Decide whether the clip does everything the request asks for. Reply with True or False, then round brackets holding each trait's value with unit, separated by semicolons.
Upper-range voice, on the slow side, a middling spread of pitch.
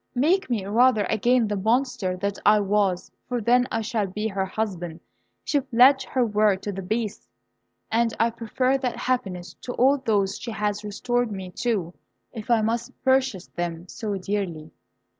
False (220 Hz; 170 wpm; 3.9 semitones)